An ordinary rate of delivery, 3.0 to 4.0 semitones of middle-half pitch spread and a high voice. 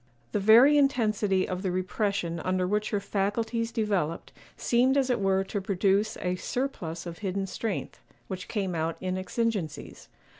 Yes: average, 155 wpm; average, 3.4 semitones; high, 200 Hz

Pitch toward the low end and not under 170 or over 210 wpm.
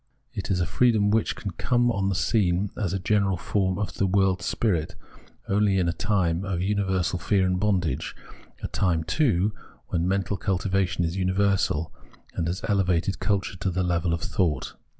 Yes: very low, 95 Hz; average, 175 wpm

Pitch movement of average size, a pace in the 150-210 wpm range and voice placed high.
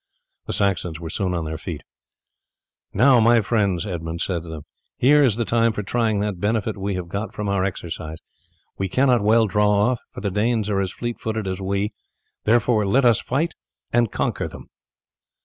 No: average, 3.6 semitones; average, 190 wpm; low, 105 Hz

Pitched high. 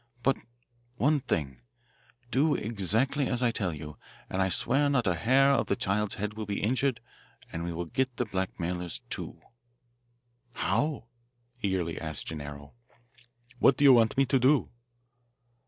No: low, 110 Hz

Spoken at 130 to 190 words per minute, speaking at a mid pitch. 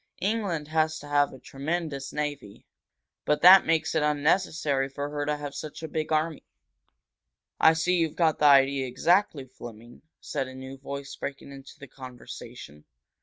Yes: average, 165 wpm; medium, 145 Hz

